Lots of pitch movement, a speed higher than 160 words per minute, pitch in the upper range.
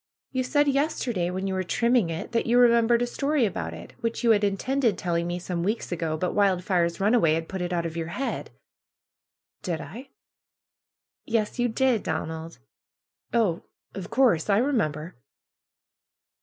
Yes: wide, 6.0 semitones; average, 170 wpm; high, 200 Hz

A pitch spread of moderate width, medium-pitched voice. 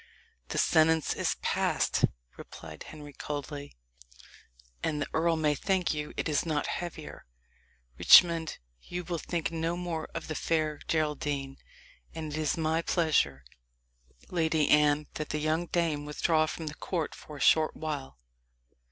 No: narrow, 1.7 semitones; medium, 155 Hz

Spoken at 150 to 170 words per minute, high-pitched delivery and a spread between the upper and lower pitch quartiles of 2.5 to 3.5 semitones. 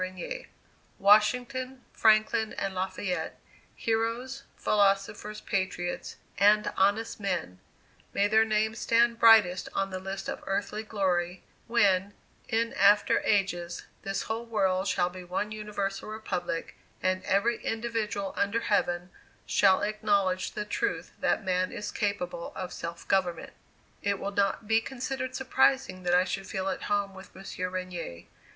No: slow, 135 wpm; high, 200 Hz; average, 2.9 semitones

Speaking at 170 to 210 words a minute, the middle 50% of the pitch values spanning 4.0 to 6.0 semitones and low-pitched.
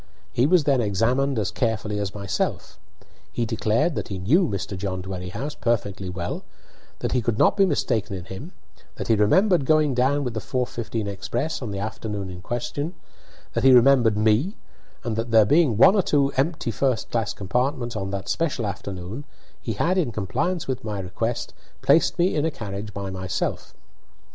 Yes: average, 180 wpm; wide, 5.6 semitones; low, 115 Hz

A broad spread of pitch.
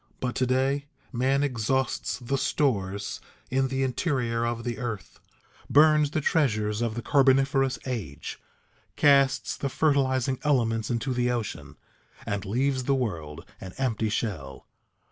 No: average, 3.4 semitones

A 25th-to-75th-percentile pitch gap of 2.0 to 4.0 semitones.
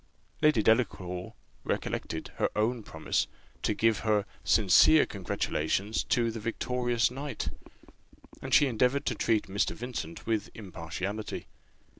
Yes: average, 3.6 semitones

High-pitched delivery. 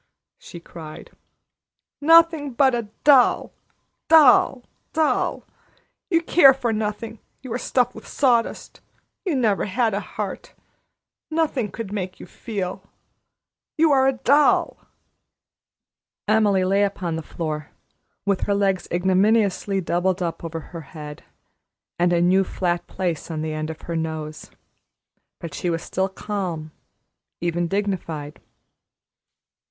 Yes: high, 195 Hz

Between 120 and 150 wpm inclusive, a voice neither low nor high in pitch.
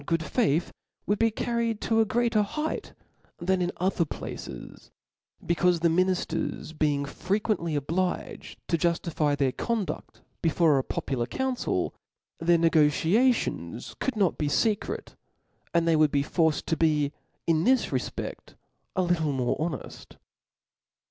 Yes: average, 140 wpm; medium, 170 Hz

